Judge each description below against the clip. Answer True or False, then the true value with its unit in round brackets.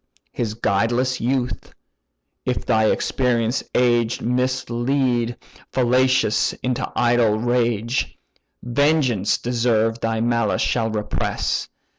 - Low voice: True (120 Hz)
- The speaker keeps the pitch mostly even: True (1.9 semitones)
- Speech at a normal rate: False (90 wpm)